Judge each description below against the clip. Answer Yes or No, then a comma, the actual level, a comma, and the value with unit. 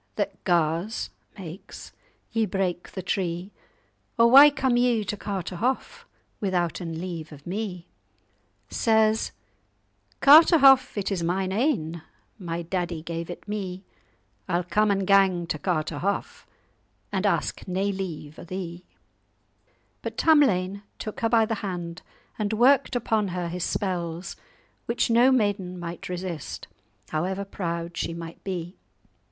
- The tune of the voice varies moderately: Yes, average, 4.0 semitones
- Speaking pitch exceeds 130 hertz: Yes, high, 190 Hz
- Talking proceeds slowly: Yes, slow, 125 wpm